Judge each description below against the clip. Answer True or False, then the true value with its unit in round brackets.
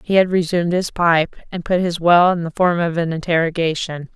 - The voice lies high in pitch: False (170 Hz)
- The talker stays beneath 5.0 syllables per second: False (5.4 syllables/s)